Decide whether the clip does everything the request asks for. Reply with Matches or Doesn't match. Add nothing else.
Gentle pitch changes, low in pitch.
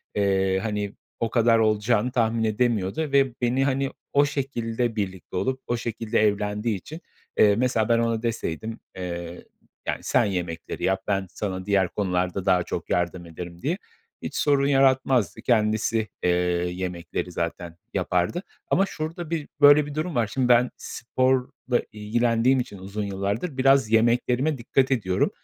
Doesn't match